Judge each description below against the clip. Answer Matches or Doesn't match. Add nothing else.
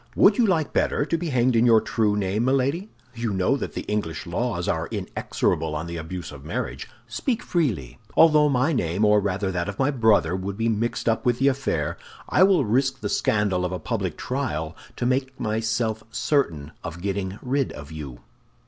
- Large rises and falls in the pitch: Matches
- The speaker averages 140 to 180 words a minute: Doesn't match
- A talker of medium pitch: Doesn't match